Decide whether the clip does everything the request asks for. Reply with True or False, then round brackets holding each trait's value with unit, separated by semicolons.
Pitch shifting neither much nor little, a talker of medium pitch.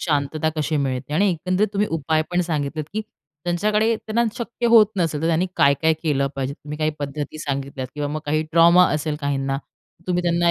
True (3.7 semitones; 155 Hz)